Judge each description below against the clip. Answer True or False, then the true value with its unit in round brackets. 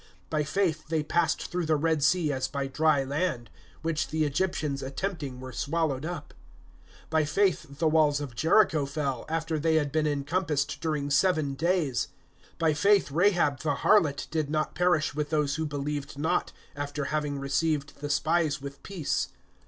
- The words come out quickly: False (165 wpm)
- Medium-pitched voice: True (150 Hz)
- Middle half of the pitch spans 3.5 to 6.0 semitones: False (2.4 semitones)